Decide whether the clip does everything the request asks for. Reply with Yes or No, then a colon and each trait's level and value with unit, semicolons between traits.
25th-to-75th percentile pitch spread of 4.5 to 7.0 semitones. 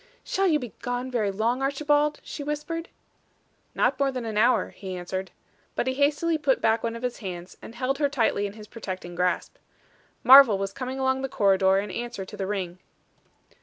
Yes: wide, 5.5 semitones